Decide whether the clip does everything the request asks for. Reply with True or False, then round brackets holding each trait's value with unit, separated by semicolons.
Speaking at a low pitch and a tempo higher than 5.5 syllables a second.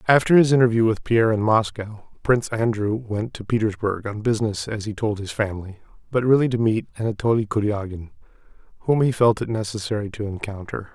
True (110 Hz; 5.9 syllables/s)